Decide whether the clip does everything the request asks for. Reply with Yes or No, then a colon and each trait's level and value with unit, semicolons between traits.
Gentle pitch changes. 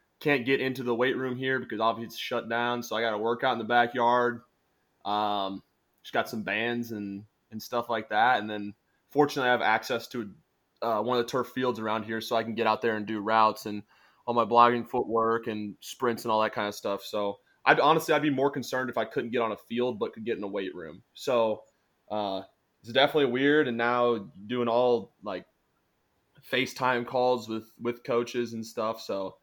Yes: narrow, 2.2 semitones